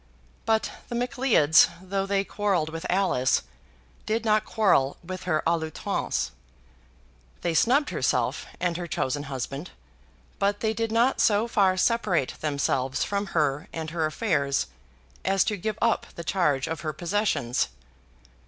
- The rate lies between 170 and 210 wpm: No, average, 145 wpm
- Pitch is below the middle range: No, medium, 180 Hz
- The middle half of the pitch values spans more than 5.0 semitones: Yes, wide, 5.6 semitones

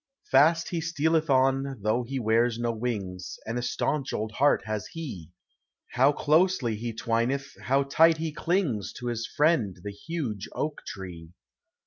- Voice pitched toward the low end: Yes, low, 130 Hz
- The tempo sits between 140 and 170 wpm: Yes, average, 155 wpm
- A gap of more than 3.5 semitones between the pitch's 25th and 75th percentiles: Yes, wide, 5.4 semitones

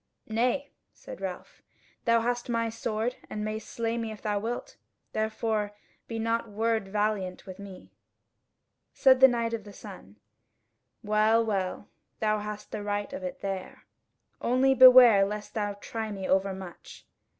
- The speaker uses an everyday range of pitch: No, narrow, 2.1 semitones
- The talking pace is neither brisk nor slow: Yes, average, 150 wpm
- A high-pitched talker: Yes, high, 220 Hz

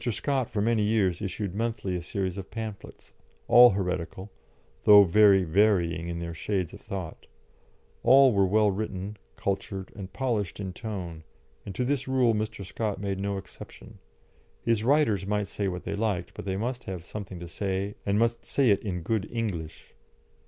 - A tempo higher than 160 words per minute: Yes, average, 175 wpm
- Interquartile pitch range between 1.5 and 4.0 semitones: Yes, average, 2.8 semitones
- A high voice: No, low, 100 Hz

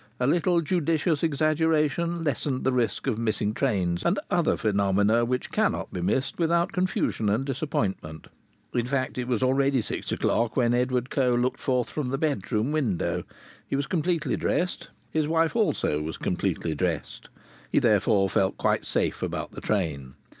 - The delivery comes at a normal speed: Yes, average, 165 wpm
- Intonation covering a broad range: Yes, wide, 6.4 semitones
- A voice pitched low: Yes, low, 130 Hz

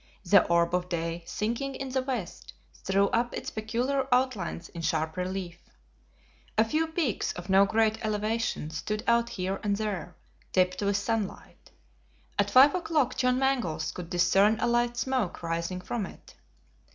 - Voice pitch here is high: Yes, high, 210 Hz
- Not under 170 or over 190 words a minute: No, average, 155 wpm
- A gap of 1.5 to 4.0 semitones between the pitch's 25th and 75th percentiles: No, average, 5.1 semitones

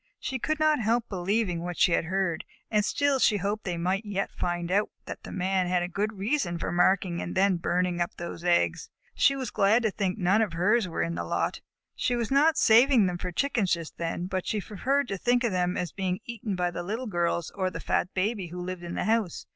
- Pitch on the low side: No, high, 190 Hz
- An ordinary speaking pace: No, fast, 240 wpm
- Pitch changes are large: No, average, 3.9 semitones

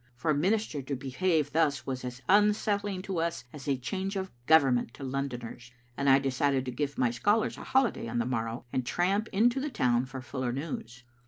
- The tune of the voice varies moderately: No, wide, 6.9 semitones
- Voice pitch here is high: No, medium, 140 Hz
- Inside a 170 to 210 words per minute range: Yes, average, 200 wpm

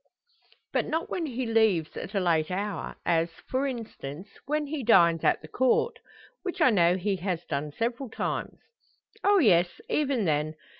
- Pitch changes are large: Yes, wide, 7.4 semitones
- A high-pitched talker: Yes, high, 205 Hz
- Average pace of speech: Yes, average, 165 wpm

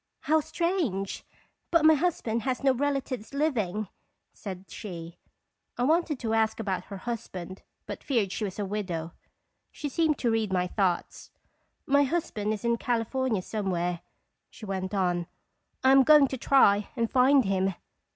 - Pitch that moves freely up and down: Yes, wide, 6.2 semitones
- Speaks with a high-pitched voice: Yes, high, 225 Hz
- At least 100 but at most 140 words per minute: No, average, 160 wpm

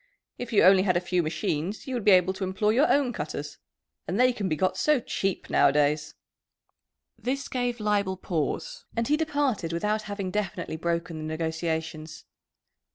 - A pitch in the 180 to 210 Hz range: Yes, high, 190 Hz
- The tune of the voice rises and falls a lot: Yes, wide, 6.2 semitones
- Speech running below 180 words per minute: Yes, average, 170 wpm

